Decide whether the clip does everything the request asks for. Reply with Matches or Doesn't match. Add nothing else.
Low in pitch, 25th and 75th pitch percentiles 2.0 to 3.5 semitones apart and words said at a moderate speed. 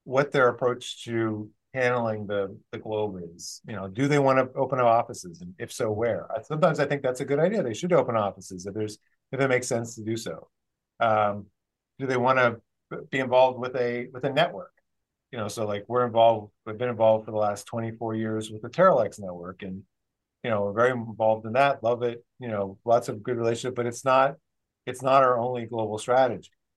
Doesn't match